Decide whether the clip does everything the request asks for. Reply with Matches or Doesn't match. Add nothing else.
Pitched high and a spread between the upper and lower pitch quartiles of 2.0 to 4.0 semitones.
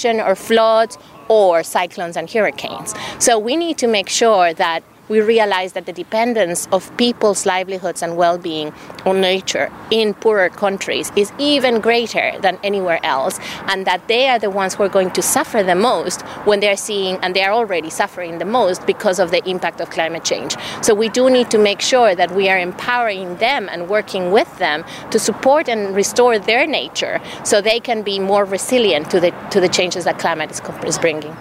Matches